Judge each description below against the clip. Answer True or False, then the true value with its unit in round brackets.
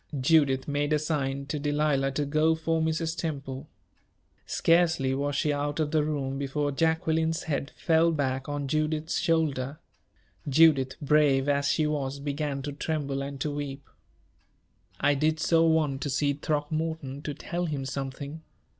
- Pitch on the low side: False (145 Hz)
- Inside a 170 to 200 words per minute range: False (155 wpm)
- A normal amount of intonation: False (2.3 semitones)